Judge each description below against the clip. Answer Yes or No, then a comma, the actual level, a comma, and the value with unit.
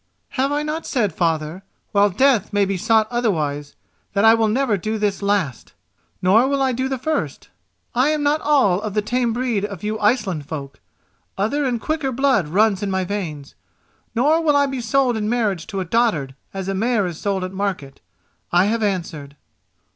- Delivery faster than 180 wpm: Yes, average, 190 wpm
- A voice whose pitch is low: No, high, 210 Hz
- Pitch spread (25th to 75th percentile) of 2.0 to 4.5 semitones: No, average, 5.2 semitones